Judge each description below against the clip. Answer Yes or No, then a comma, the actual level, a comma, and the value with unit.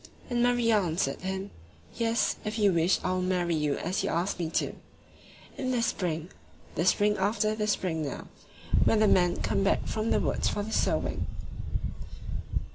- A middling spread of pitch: Yes, average, 3.8 semitones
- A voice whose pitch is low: No, high, 195 Hz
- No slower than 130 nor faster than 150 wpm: No, average, 175 wpm